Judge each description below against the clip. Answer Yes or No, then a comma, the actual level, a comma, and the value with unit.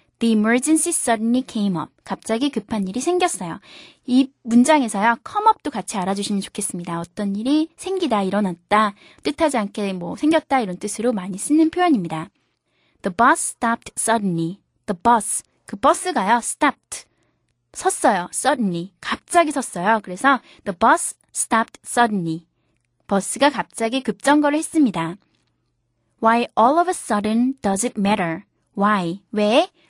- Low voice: No, high, 230 Hz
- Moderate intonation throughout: No, wide, 6.3 semitones